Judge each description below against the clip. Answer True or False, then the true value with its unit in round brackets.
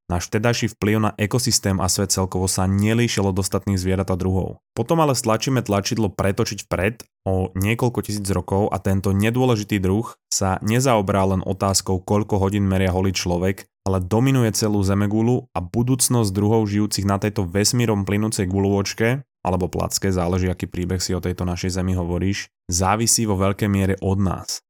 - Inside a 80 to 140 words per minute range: False (165 wpm)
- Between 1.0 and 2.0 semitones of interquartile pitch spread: False (2.7 semitones)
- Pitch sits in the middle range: False (100 Hz)